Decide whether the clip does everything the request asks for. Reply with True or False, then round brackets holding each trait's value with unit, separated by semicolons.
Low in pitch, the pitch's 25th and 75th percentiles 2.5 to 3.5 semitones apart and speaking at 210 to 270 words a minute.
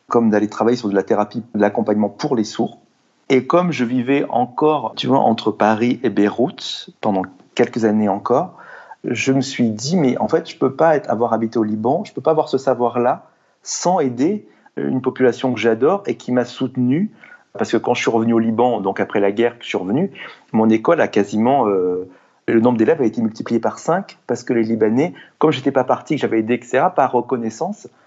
True (120 Hz; 3.0 semitones; 220 wpm)